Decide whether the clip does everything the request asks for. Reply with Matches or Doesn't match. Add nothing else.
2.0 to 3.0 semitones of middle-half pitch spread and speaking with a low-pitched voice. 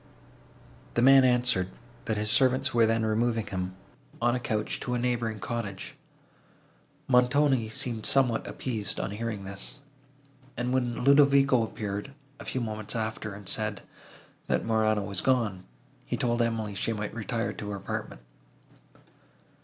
Matches